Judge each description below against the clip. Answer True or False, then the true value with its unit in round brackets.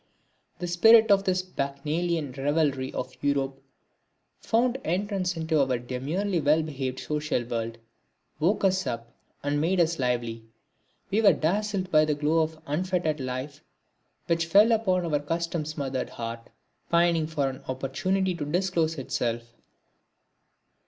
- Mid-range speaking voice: True (155 Hz)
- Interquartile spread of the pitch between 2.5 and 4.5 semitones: False (5.1 semitones)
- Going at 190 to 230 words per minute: False (135 wpm)